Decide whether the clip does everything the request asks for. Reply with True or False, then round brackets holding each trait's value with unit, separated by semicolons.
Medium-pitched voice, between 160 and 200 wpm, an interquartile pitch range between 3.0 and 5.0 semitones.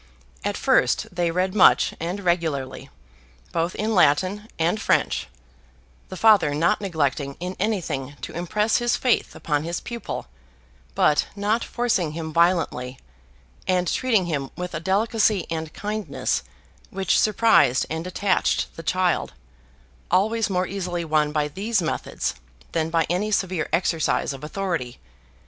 False (180 Hz; 135 wpm; 4.2 semitones)